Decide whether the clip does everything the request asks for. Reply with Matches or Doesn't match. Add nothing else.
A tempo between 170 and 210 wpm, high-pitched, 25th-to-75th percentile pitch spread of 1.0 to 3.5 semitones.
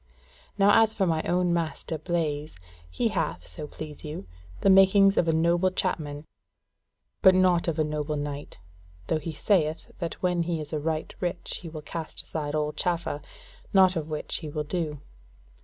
Doesn't match